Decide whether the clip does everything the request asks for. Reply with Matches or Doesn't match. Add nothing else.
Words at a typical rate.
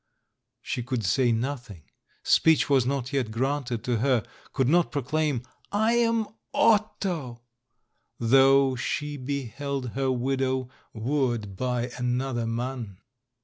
Doesn't match